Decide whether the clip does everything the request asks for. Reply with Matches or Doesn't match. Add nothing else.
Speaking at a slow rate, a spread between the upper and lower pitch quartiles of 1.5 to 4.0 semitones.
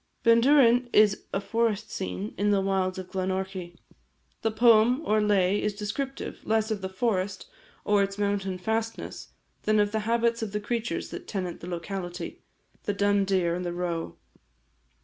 Doesn't match